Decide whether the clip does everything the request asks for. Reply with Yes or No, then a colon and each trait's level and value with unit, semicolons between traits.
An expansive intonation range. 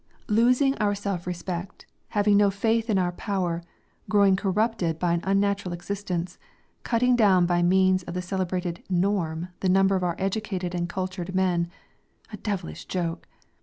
No: narrow, 2.5 semitones